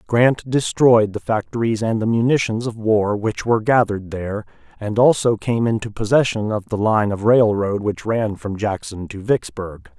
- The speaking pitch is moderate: No, low, 110 Hz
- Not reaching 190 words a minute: Yes, average, 175 wpm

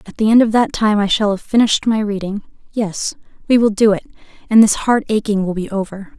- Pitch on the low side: No, high, 210 Hz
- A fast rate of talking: Yes, fast, 225 wpm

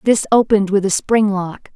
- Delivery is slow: No, fast, 205 wpm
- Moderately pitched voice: No, high, 205 Hz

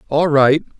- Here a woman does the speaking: No, male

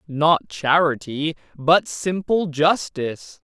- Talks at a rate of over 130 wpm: No, slow, 85 wpm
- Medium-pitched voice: Yes, medium, 155 Hz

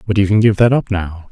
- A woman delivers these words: No, male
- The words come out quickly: Yes, fast, 320 wpm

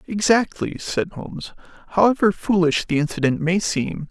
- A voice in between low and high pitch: Yes, medium, 180 Hz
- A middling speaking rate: No, slow, 130 wpm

